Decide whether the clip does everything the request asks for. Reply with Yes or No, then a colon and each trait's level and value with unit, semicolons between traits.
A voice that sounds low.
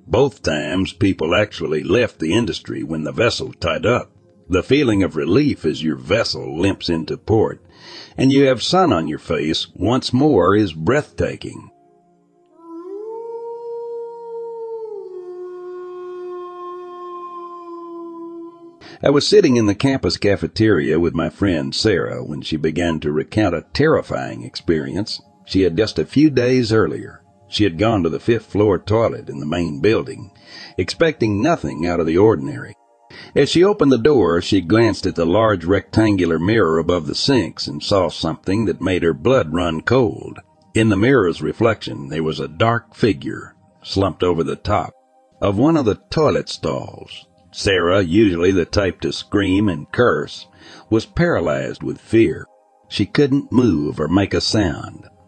Yes: low, 115 Hz